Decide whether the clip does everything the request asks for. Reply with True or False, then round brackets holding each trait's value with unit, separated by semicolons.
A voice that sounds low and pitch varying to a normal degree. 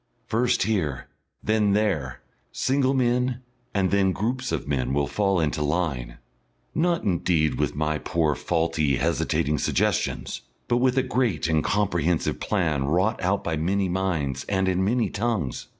False (95 Hz; 6.1 semitones)